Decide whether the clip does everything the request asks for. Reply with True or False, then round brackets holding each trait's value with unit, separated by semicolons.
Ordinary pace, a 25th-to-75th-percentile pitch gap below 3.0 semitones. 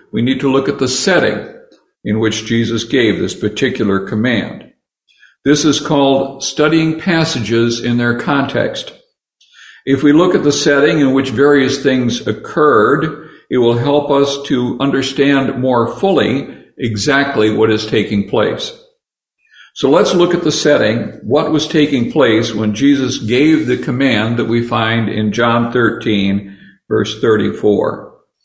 False (145 wpm; 4.1 semitones)